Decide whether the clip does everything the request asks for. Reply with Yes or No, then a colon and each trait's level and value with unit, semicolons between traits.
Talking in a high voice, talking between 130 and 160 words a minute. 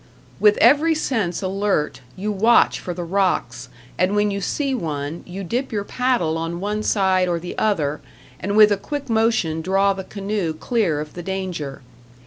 No: high, 195 Hz; average, 175 wpm